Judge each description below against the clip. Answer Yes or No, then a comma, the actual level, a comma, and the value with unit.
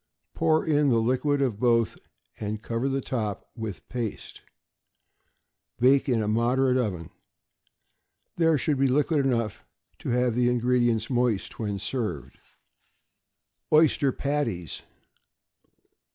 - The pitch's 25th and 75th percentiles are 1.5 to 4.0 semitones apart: Yes, average, 3.5 semitones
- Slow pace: Yes, slow, 115 wpm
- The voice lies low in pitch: Yes, low, 125 Hz